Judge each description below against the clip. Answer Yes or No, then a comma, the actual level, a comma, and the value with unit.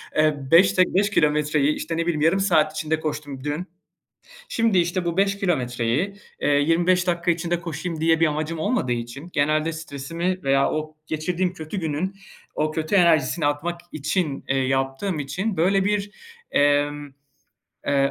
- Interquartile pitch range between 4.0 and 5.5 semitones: No, average, 3.4 semitones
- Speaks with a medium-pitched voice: Yes, medium, 160 Hz